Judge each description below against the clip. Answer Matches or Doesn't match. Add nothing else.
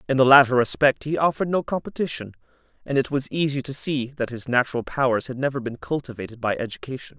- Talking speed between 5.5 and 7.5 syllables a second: Matches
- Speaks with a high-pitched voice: Doesn't match